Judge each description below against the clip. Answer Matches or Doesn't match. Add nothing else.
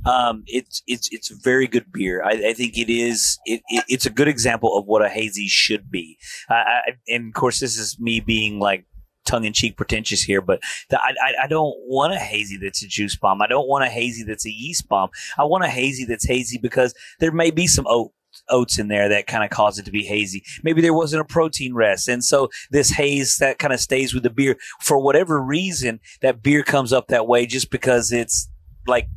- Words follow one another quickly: Matches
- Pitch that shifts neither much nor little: Matches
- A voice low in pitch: Matches